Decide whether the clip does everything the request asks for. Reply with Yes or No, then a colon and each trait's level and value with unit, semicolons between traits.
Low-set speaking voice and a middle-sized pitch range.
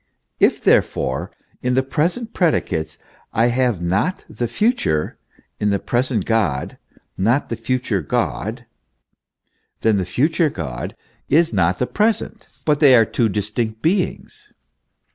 No: low, 120 Hz; wide, 7.4 semitones